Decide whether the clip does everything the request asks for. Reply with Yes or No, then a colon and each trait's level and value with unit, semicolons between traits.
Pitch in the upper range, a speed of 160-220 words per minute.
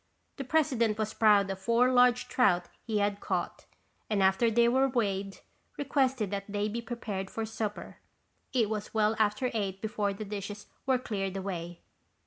Yes: high, 215 Hz; average, 165 wpm